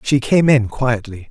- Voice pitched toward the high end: No, low, 125 Hz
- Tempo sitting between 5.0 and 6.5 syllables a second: No, 4.2 syllables/s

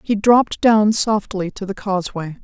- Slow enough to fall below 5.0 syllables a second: Yes, 4.8 syllables/s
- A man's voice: No, female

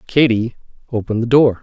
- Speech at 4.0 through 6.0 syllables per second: No, 6.2 syllables/s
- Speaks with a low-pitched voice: Yes, low, 120 Hz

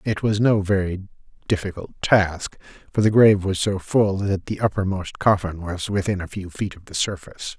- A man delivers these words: Yes, male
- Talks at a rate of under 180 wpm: No, average, 190 wpm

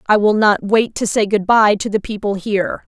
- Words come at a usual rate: No, fast, 245 wpm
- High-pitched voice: Yes, high, 210 Hz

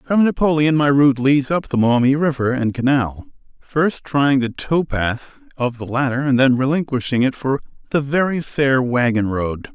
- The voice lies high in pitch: No, low, 135 Hz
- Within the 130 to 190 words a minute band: Yes, average, 180 wpm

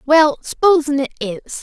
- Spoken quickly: No, average, 150 wpm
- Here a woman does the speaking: Yes, female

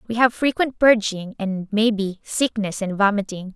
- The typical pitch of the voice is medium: No, high, 210 Hz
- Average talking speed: Yes, average, 150 wpm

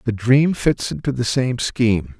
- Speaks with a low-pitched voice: Yes, low, 120 Hz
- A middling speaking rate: Yes, average, 190 wpm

